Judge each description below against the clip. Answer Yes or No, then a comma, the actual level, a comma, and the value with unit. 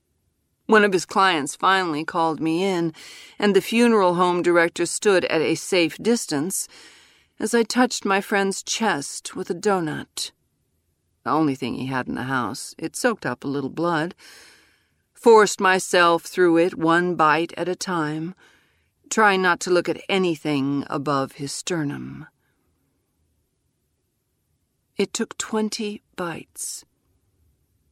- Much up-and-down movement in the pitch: Yes, wide, 5.7 semitones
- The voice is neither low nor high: Yes, medium, 170 Hz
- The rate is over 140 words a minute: No, slow, 135 wpm